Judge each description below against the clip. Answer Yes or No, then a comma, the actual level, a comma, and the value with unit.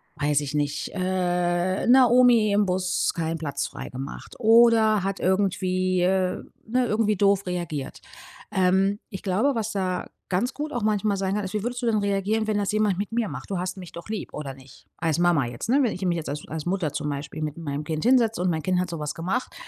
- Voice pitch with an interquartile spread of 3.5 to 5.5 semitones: Yes, average, 4.2 semitones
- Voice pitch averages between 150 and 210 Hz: Yes, medium, 185 Hz